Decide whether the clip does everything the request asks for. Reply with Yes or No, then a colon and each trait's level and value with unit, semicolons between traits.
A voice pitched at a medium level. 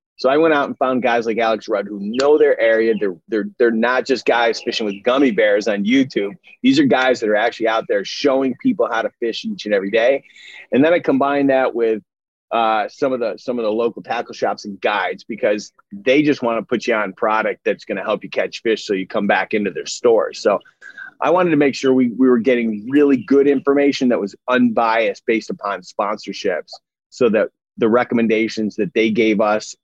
No: low, 125 Hz